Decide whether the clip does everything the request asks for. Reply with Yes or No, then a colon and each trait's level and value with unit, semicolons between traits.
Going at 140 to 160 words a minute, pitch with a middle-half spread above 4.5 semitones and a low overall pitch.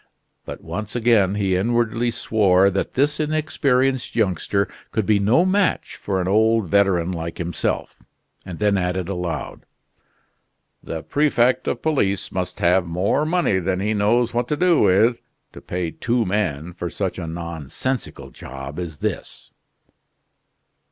Yes: average, 145 wpm; average, 5.0 semitones; low, 100 Hz